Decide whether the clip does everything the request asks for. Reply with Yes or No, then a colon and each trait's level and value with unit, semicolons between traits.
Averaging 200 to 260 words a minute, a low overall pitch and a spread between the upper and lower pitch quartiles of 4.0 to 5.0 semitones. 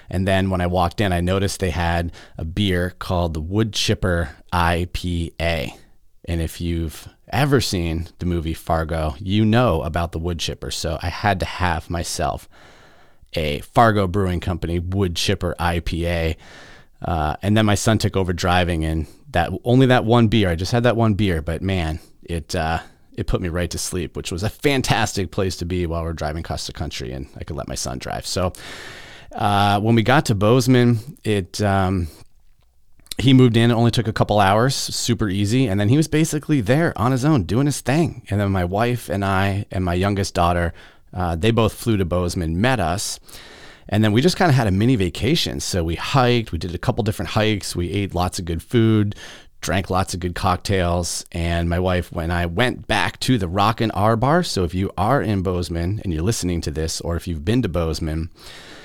Yes: fast, 205 wpm; very low, 95 Hz; average, 4.6 semitones